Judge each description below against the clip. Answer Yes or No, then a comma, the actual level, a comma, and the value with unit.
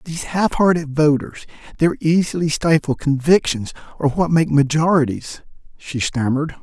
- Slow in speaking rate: Yes, slow, 125 wpm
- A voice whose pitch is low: No, medium, 155 Hz